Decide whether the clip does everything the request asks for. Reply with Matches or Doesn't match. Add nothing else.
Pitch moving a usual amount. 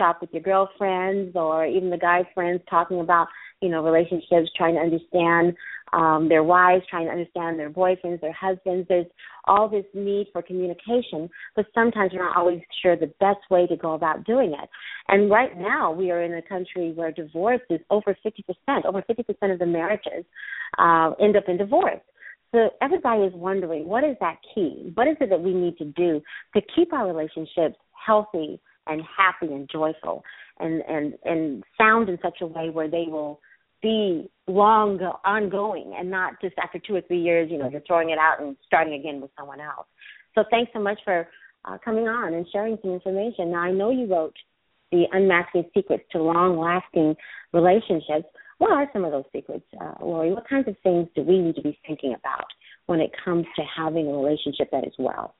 Matches